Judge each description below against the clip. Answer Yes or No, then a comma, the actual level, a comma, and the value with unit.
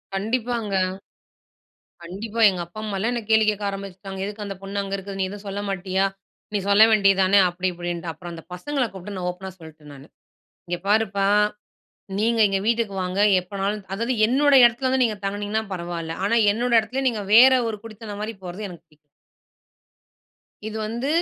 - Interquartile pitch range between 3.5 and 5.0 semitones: No, average, 3.0 semitones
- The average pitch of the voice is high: Yes, high, 200 Hz